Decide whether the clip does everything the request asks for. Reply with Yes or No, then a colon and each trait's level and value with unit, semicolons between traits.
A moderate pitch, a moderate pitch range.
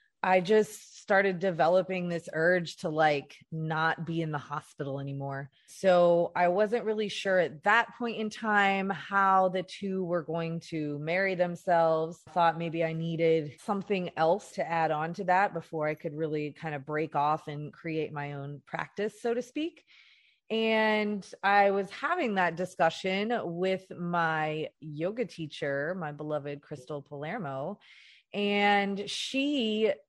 Yes: medium, 175 Hz; average, 4.2 semitones